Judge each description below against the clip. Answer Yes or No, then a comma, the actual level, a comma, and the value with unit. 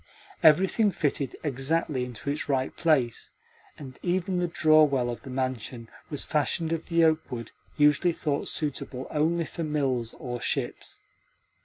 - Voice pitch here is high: No, medium, 145 Hz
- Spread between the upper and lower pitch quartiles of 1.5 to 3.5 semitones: No, average, 4.0 semitones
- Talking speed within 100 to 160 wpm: Yes, average, 145 wpm